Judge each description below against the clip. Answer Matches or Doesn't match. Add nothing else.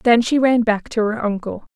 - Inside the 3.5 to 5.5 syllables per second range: Matches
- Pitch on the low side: Doesn't match